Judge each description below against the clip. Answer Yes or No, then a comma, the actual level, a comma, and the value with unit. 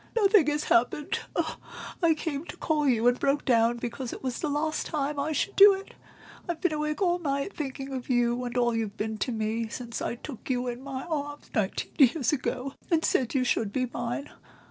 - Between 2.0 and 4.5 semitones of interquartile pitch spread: Yes, average, 4.1 semitones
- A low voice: No, very high, 270 Hz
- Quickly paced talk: Yes, fast, 210 wpm